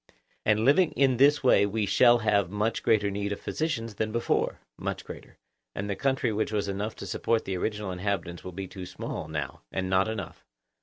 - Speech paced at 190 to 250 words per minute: Yes, average, 200 wpm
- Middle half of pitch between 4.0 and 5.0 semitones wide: No, average, 2.9 semitones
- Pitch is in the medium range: No, low, 105 Hz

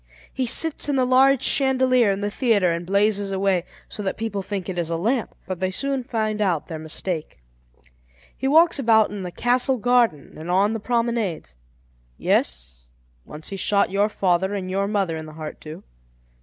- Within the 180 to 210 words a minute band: Yes, average, 185 wpm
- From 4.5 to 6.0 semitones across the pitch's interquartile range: Yes, average, 5.2 semitones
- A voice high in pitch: Yes, high, 200 Hz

